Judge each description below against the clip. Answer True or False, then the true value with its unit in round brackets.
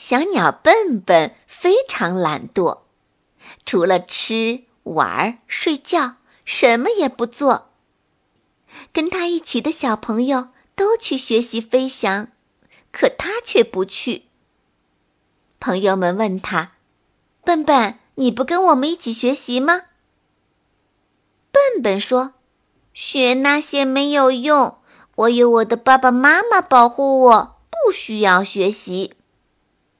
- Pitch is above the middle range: True (255 Hz)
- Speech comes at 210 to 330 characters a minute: False (160 characters per minute)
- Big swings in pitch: False (4.9 semitones)